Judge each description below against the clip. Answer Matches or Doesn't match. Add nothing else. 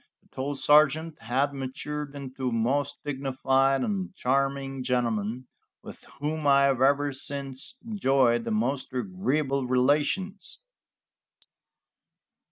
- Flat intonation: Matches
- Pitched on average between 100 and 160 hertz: Matches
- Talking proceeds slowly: Matches